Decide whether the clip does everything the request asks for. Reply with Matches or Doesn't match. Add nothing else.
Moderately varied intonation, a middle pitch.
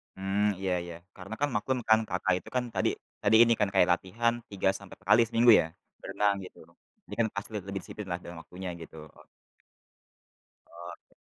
Doesn't match